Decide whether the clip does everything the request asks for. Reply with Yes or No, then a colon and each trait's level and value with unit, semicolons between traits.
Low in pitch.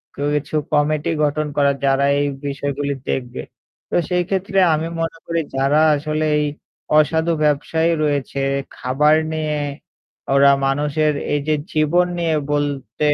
No: medium, 150 Hz